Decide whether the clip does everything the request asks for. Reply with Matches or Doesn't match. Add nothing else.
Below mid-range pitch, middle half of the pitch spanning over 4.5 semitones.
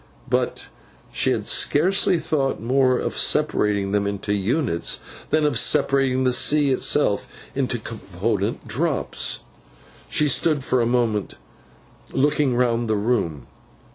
Matches